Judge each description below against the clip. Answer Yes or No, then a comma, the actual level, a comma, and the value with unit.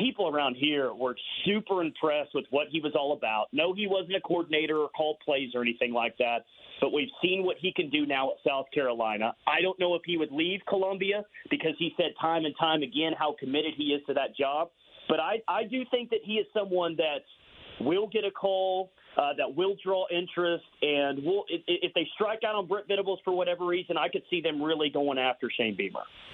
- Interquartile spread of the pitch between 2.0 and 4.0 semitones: No, average, 4.5 semitones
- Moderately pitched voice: Yes, medium, 170 Hz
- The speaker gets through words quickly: Yes, fast, 225 wpm